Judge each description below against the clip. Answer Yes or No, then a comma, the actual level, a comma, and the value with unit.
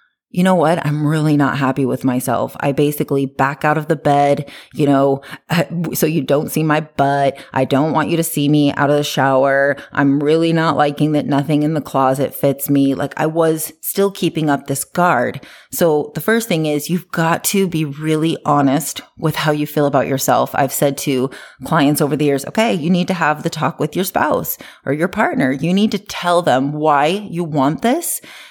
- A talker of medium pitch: Yes, medium, 150 Hz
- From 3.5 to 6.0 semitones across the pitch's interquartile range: No, average, 2.9 semitones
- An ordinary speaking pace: No, fast, 210 wpm